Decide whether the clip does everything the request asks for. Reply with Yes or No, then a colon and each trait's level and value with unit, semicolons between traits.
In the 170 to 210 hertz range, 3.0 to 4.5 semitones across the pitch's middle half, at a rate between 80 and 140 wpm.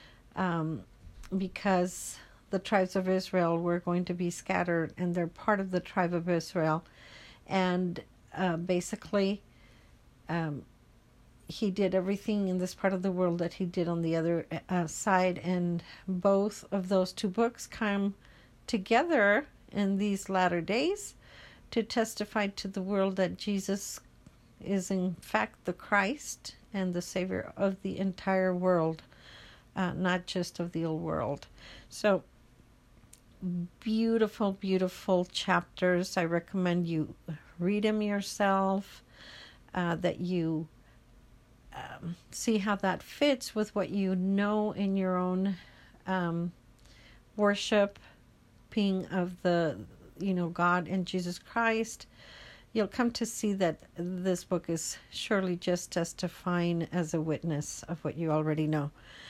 No: medium, 185 Hz; narrow, 2.6 semitones; slow, 135 wpm